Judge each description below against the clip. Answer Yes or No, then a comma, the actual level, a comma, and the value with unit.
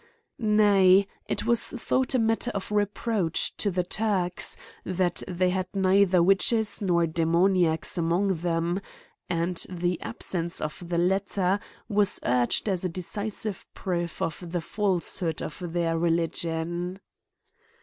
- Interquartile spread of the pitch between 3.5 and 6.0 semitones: No, average, 2.8 semitones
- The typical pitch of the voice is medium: Yes, medium, 180 Hz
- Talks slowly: Yes, slow, 130 wpm